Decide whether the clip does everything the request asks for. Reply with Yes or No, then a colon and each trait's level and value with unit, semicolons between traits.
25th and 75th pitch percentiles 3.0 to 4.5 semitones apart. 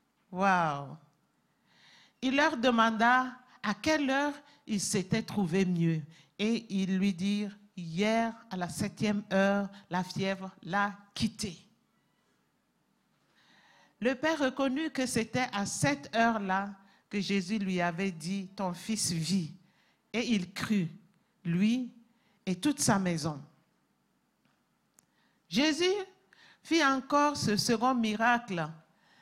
Yes: average, 3.8 semitones